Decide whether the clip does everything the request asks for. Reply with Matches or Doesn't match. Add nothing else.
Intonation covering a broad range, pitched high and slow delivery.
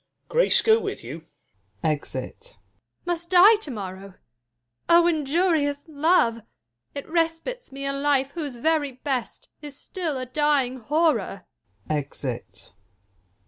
Matches